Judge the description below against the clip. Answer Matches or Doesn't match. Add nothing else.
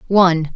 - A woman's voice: Matches